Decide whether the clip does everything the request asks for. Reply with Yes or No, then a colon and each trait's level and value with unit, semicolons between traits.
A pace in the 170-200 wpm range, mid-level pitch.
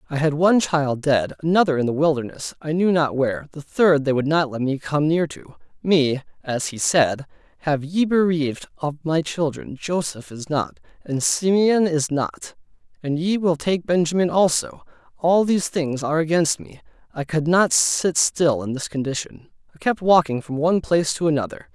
Yes: average, 190 wpm; medium, 155 Hz